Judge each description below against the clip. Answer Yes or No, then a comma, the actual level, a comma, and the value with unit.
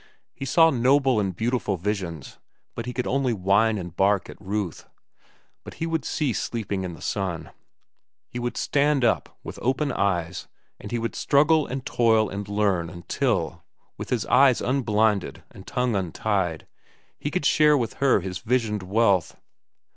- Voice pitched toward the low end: Yes, low, 110 Hz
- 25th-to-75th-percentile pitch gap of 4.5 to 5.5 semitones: Yes, average, 5.1 semitones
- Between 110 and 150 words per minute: No, average, 160 wpm